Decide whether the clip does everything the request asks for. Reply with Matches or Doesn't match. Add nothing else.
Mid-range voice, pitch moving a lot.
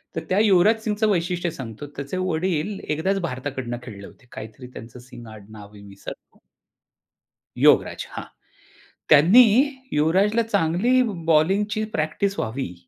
Matches